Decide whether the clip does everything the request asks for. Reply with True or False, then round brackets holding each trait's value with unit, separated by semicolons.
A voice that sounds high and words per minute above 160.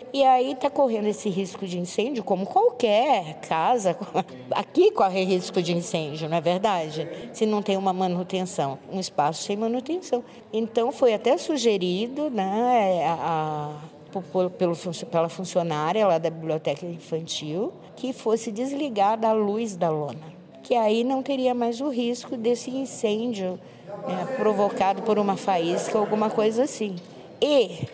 False (205 Hz; 150 wpm)